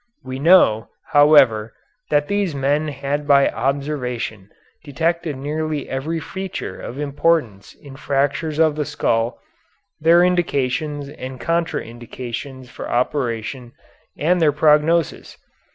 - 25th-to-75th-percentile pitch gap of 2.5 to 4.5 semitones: Yes, average, 3.4 semitones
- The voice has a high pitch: No, medium, 145 Hz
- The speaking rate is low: Yes, slow, 115 wpm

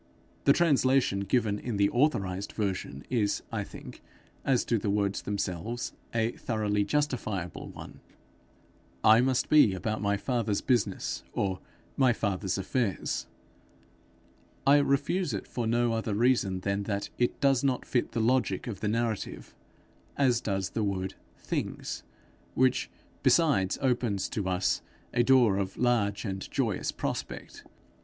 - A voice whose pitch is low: Yes, low, 110 Hz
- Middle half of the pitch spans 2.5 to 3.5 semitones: No, average, 4.1 semitones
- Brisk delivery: No, average, 140 wpm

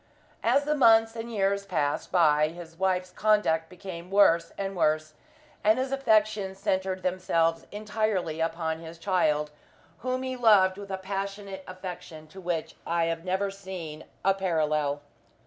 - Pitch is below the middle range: No, medium, 185 Hz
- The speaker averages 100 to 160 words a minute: Yes, average, 145 wpm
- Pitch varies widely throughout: No, average, 3.6 semitones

